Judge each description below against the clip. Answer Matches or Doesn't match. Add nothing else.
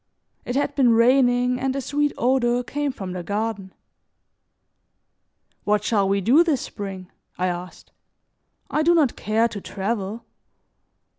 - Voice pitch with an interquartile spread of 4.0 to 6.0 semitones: Matches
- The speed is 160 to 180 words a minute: Doesn't match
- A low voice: Doesn't match